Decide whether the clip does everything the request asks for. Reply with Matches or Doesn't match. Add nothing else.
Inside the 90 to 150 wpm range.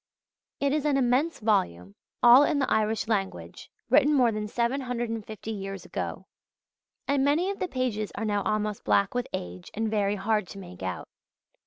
Doesn't match